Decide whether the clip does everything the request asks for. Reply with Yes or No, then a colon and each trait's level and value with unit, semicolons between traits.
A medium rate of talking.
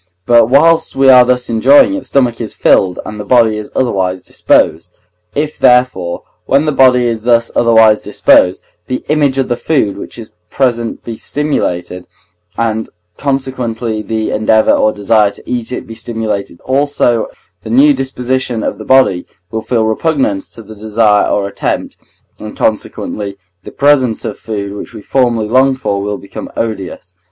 Yes: average, 170 wpm